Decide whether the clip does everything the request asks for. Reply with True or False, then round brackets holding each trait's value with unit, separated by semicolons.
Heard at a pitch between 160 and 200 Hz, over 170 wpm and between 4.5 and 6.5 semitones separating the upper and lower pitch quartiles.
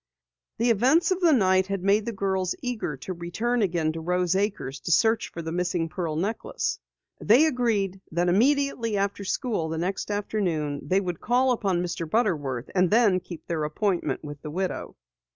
True (190 Hz; 180 wpm; 4.8 semitones)